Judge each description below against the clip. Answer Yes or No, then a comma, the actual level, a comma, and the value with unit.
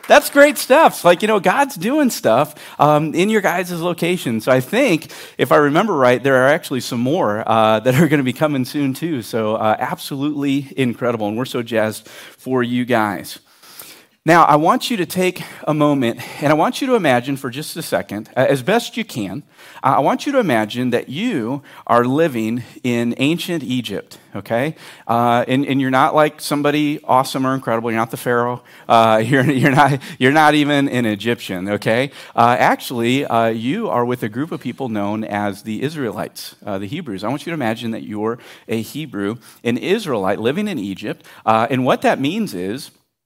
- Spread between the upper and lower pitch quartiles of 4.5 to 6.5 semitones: Yes, average, 4.9 semitones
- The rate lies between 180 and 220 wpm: Yes, average, 200 wpm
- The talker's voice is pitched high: No, low, 130 Hz